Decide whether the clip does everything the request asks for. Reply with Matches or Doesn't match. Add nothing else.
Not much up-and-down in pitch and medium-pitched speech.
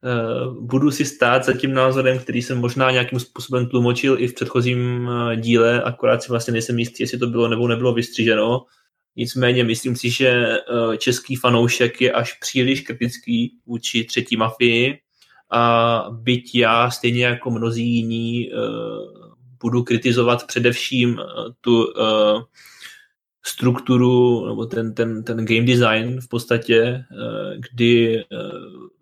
Doesn't match